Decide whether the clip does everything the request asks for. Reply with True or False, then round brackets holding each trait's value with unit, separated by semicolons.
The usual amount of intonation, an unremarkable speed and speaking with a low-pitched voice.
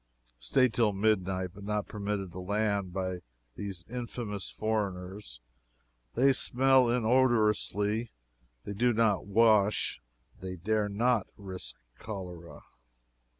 False (3.1 semitones; 110 wpm; 105 Hz)